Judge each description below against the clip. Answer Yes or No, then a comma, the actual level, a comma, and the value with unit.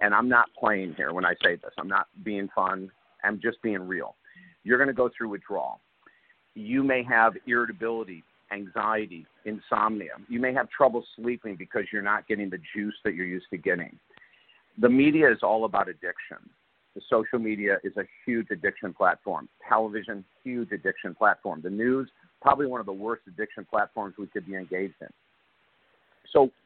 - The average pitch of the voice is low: Yes, low, 110 Hz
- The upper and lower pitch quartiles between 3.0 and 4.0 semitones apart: Yes, average, 3.4 semitones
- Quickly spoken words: No, average, 175 wpm